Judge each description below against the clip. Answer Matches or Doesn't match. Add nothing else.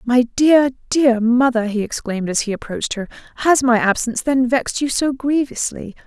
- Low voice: Doesn't match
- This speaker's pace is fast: Doesn't match